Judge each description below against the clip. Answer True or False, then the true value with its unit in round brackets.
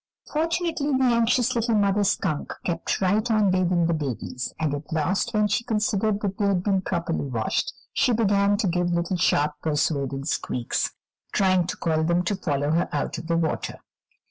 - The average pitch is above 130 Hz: True (185 Hz)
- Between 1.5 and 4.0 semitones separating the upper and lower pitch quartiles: False (4.8 semitones)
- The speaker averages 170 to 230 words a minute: True (180 wpm)